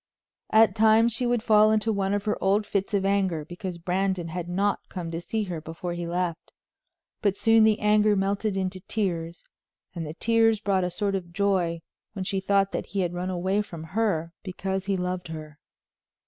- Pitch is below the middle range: No, high, 195 Hz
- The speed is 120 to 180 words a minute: No, average, 195 wpm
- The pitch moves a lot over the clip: No, average, 3.1 semitones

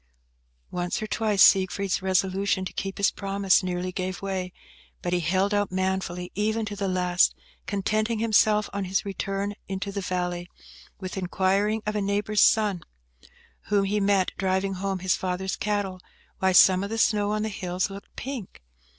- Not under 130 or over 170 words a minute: Yes, average, 165 wpm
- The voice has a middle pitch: No, high, 195 Hz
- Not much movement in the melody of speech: Yes, narrow, 1.8 semitones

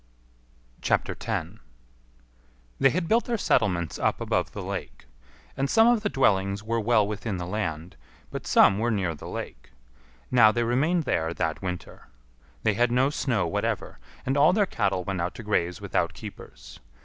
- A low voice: Yes, low, 110 Hz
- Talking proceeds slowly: No, average, 165 wpm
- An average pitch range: No, wide, 6.9 semitones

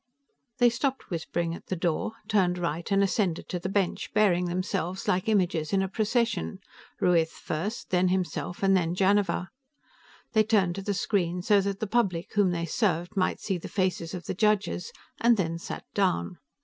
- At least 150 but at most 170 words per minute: No, average, 185 wpm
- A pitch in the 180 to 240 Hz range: Yes, medium, 185 Hz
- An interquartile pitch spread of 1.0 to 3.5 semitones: Yes, average, 2.8 semitones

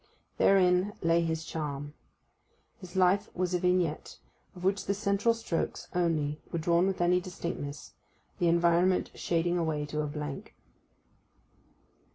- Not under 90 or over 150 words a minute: Yes, slow, 135 wpm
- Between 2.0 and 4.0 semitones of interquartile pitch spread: Yes, narrow, 2.4 semitones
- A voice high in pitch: No, medium, 175 Hz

